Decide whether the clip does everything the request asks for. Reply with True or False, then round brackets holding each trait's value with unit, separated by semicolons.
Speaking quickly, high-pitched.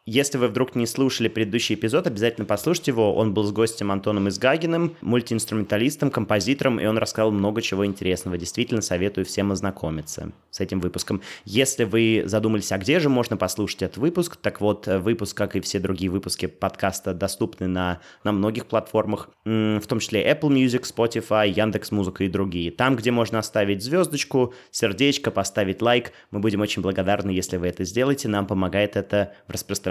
False (170 wpm; 105 Hz)